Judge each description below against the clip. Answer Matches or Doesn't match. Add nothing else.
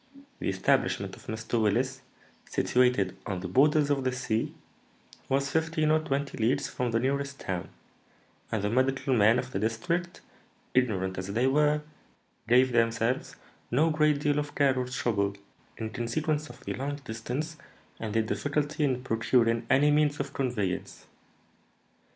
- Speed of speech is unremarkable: Matches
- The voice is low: Matches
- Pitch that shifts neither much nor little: Matches